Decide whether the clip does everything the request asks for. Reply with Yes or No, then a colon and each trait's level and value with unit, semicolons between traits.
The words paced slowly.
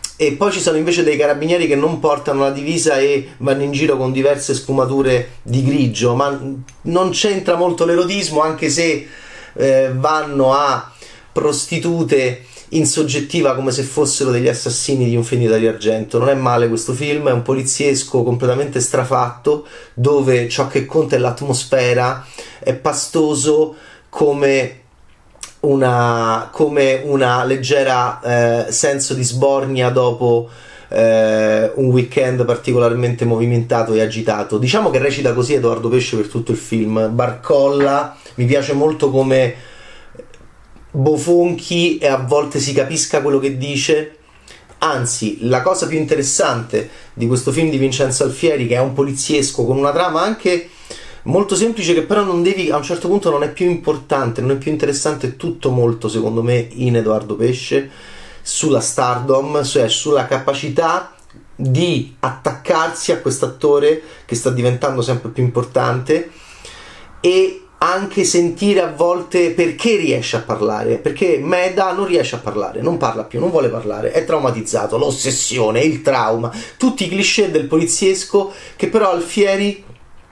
No: average, 145 wpm